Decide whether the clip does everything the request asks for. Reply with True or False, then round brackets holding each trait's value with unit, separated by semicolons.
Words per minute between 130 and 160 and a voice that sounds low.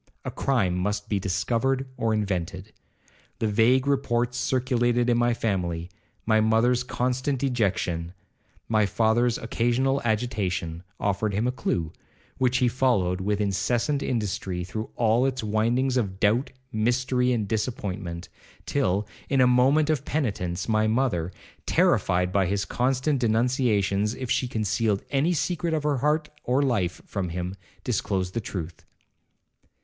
True (140 wpm; 115 Hz)